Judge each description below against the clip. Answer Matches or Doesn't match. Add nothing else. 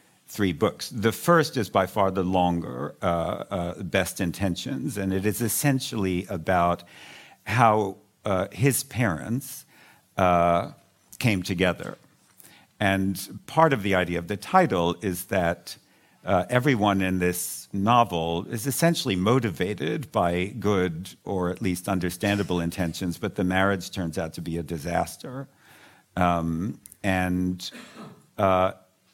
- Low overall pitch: Matches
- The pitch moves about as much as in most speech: Matches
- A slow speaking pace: Matches